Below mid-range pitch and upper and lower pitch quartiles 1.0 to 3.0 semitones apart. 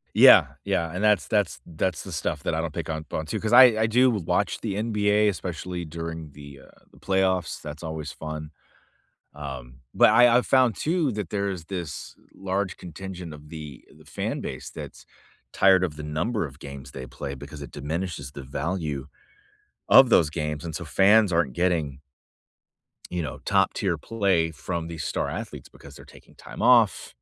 No: very low, 85 Hz; average, 4.5 semitones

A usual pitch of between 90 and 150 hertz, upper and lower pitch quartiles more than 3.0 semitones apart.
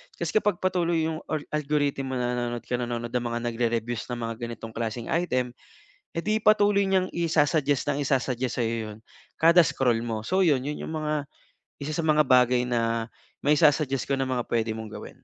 Yes: low, 135 Hz; average, 4.9 semitones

